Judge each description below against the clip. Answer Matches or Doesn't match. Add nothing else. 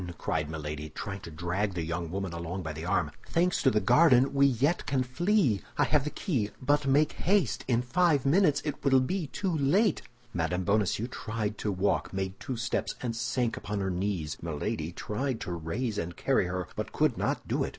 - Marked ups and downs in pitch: Matches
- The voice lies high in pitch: Doesn't match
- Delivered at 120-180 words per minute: Doesn't match